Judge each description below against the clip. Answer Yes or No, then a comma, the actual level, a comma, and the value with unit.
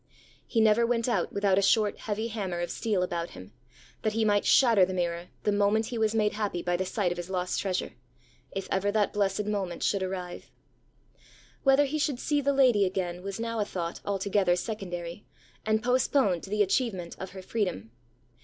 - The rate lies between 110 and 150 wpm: No, average, 195 wpm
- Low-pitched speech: No, high, 200 Hz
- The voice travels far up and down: No, average, 3.3 semitones